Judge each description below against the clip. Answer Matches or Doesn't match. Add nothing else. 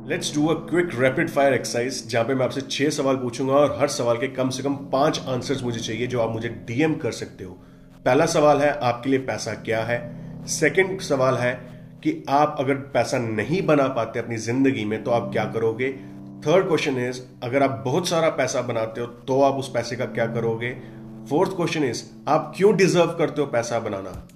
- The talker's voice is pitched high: Doesn't match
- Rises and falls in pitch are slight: Doesn't match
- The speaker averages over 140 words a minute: Matches